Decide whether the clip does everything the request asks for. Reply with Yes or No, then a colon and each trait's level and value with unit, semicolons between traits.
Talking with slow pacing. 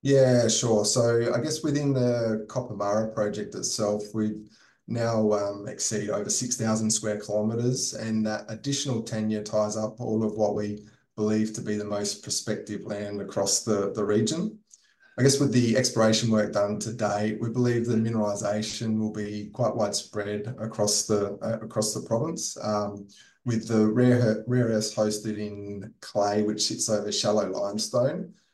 No: average, 160 wpm